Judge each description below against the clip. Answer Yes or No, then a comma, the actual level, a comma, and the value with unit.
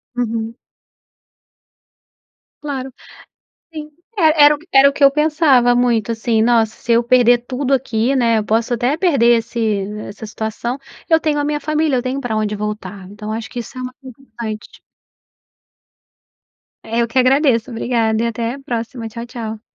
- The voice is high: Yes, high, 240 Hz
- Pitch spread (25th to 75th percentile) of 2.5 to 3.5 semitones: Yes, average, 3.2 semitones